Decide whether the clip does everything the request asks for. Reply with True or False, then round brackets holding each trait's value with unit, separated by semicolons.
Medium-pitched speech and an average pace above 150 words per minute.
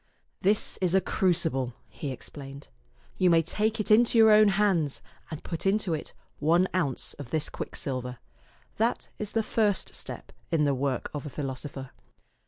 True (165 Hz; 175 wpm)